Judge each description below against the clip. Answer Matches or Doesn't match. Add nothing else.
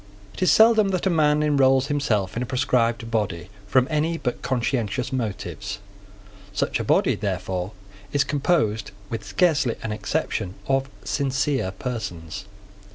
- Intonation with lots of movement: Matches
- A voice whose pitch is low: Matches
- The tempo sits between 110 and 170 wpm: Matches